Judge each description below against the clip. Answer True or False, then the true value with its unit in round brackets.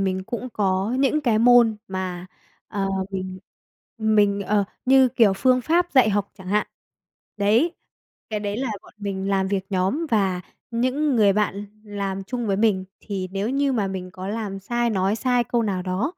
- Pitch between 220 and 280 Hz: False (205 Hz)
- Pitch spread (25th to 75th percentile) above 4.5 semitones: False (3.8 semitones)